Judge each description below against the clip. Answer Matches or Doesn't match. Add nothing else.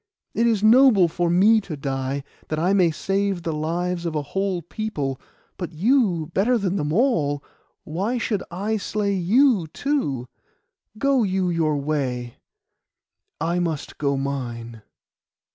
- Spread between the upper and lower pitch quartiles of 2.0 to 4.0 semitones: Doesn't match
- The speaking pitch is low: Doesn't match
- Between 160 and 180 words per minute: Doesn't match